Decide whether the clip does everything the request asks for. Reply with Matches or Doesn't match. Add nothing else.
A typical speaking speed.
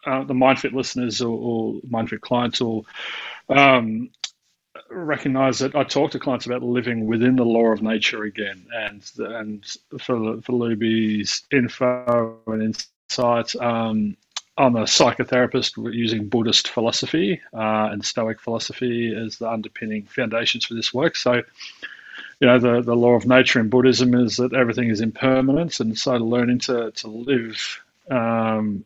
Matches